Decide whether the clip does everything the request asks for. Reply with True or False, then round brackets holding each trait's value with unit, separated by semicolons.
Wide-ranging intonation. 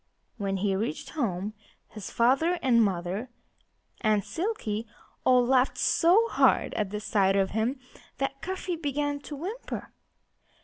True (6.0 semitones)